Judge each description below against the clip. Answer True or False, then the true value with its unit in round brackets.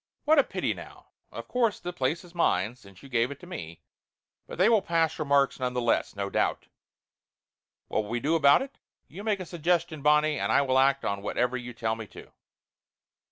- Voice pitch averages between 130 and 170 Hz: True (140 Hz)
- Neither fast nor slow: False (210 wpm)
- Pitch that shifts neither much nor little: False (6.4 semitones)